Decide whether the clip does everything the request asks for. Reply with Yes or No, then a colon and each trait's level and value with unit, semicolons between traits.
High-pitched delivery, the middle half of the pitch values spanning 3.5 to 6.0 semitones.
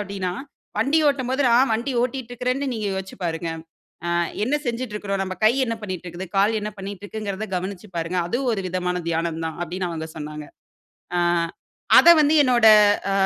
Yes: high, 200 Hz; average, 4.9 semitones